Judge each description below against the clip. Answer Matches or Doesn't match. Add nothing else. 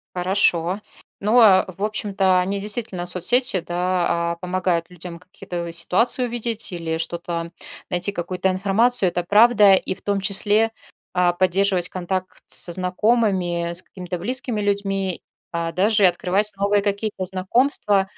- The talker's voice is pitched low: Doesn't match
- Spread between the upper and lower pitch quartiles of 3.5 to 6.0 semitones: Doesn't match